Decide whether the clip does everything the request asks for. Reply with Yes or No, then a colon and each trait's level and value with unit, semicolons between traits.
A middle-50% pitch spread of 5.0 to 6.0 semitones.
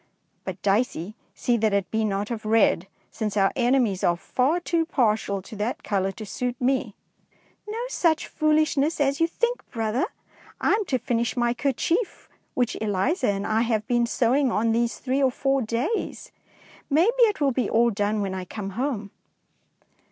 No: average, 4.6 semitones